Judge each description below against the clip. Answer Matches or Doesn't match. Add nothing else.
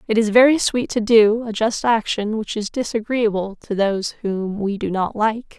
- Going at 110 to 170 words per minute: Doesn't match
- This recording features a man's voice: Doesn't match